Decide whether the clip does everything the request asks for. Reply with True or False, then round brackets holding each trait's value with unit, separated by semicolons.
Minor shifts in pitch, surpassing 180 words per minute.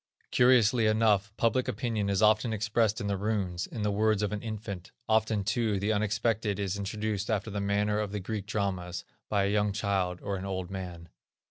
True (1.8 semitones; 195 wpm)